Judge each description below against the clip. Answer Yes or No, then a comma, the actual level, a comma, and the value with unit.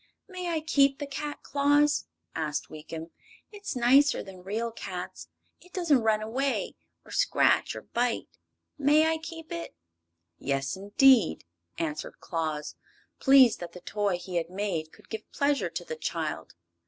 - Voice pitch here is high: Yes, high, 235 Hz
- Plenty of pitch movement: Yes, wide, 8.4 semitones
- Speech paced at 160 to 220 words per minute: No, average, 150 wpm